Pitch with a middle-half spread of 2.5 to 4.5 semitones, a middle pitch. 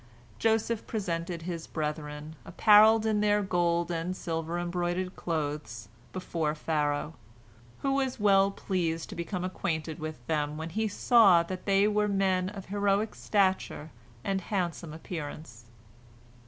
Yes: average, 4.0 semitones; medium, 175 Hz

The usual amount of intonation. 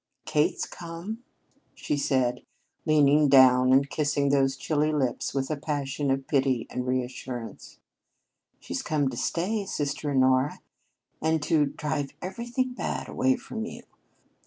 Yes: average, 3.1 semitones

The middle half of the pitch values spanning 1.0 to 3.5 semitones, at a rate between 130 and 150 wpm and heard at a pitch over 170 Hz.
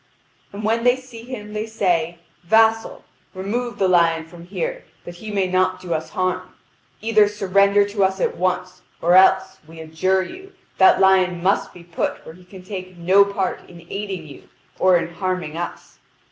No: average, 2.9 semitones; average, 180 wpm; high, 190 Hz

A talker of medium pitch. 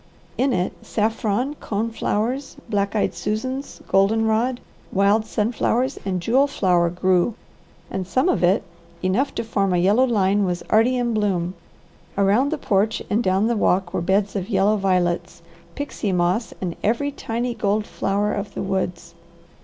No: high, 205 Hz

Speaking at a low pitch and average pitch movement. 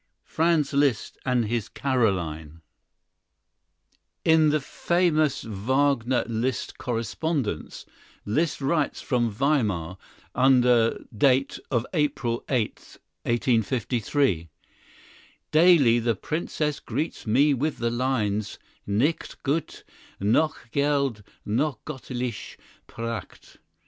Yes: low, 125 Hz; average, 4.4 semitones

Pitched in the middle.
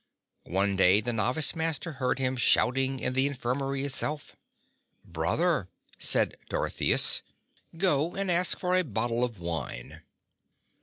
No: low, 130 Hz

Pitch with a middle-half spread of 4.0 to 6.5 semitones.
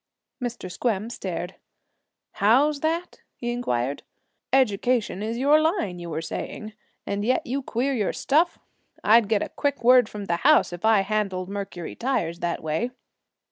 Yes: wide, 5.4 semitones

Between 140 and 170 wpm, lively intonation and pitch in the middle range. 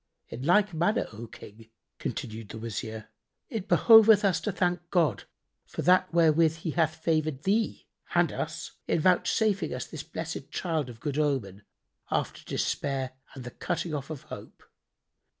Yes: average, 155 wpm; wide, 5.8 semitones; medium, 160 Hz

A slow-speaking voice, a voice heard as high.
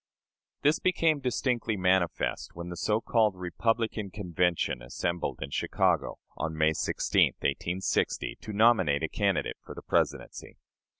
No: slow, 130 wpm; very low, 95 Hz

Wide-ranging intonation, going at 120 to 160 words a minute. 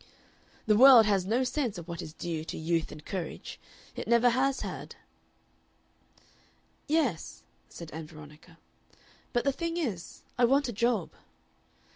Yes: wide, 7.4 semitones; average, 145 wpm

